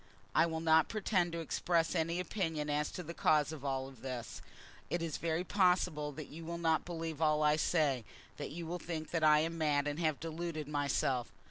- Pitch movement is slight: Yes, narrow, 2.1 semitones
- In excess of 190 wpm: Yes, fast, 205 wpm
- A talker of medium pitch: Yes, medium, 160 Hz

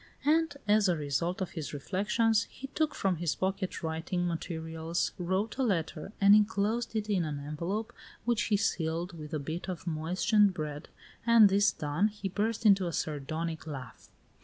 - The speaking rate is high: No, average, 170 wpm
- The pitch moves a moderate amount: Yes, average, 4.5 semitones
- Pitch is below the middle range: No, medium, 185 Hz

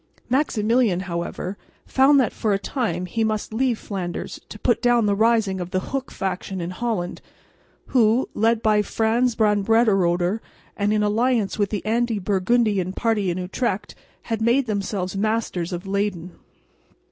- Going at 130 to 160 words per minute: Yes, average, 155 wpm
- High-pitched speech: Yes, high, 210 Hz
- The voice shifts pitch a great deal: No, average, 3.5 semitones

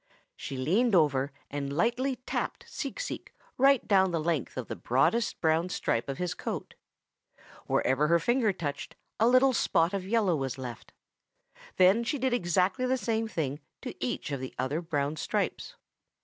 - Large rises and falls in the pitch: Yes, wide, 8.4 semitones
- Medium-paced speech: Yes, average, 165 wpm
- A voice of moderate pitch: Yes, medium, 175 Hz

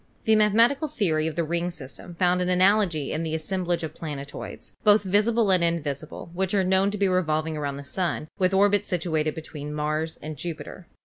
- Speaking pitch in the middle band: Yes, medium, 175 Hz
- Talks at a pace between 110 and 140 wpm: No, average, 190 wpm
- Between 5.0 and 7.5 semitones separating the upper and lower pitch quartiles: No, average, 3.7 semitones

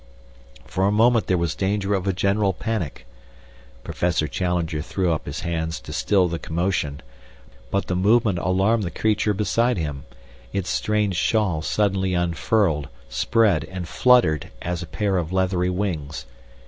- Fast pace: No, average, 150 wpm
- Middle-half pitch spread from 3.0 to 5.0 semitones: Yes, average, 3.5 semitones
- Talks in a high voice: No, very low, 95 Hz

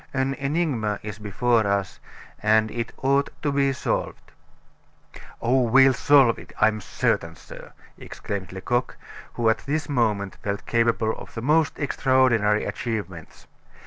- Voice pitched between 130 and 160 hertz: No, low, 115 Hz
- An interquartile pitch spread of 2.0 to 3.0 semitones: No, average, 4.2 semitones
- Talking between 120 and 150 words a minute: Yes, average, 140 wpm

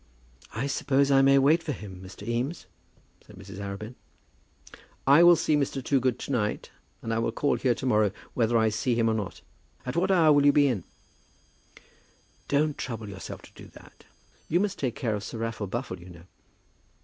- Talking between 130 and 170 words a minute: No, average, 195 wpm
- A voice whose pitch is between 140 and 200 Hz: No, low, 125 Hz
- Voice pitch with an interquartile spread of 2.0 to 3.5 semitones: No, average, 4.9 semitones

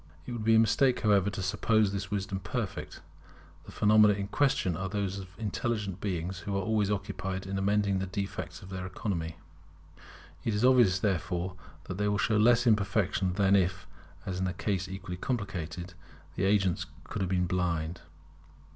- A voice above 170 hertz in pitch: No, very low, 95 Hz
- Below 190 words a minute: Yes, average, 175 wpm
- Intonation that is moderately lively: No, narrow, 2.2 semitones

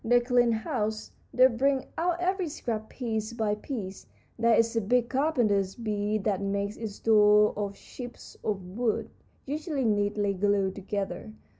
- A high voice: Yes, high, 220 Hz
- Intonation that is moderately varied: Yes, average, 3.1 semitones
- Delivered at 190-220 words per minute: No, average, 150 wpm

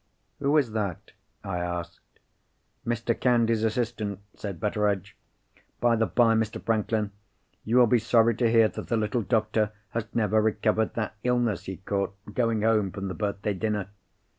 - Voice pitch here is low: Yes, low, 110 Hz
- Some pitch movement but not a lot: No, narrow, 2.2 semitones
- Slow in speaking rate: No, average, 160 wpm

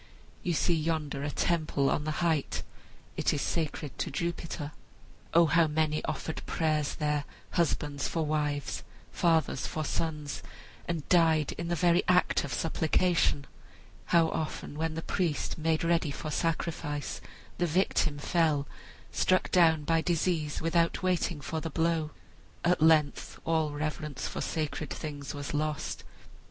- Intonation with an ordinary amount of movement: No, narrow, 2.1 semitones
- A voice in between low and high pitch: Yes, medium, 160 Hz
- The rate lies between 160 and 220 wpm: No, average, 145 wpm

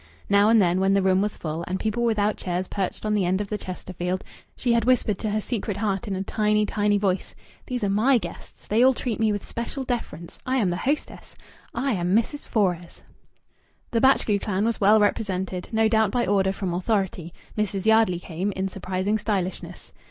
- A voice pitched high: Yes, high, 205 Hz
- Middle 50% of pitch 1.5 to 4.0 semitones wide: Yes, average, 2.9 semitones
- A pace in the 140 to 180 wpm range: No, fast, 205 wpm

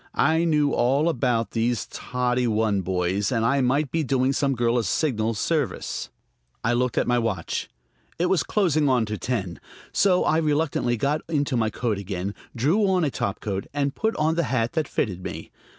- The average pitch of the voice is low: Yes, low, 125 Hz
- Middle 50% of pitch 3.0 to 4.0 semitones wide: No, average, 5.2 semitones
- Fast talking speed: No, average, 185 wpm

